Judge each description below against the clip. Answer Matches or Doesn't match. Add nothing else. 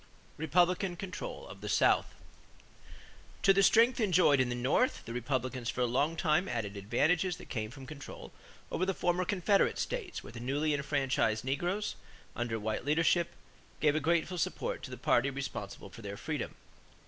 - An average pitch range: Doesn't match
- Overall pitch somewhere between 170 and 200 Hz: Doesn't match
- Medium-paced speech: Matches